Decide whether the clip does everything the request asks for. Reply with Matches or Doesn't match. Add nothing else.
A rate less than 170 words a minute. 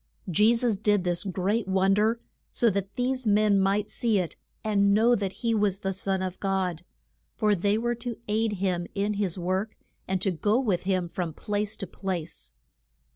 Doesn't match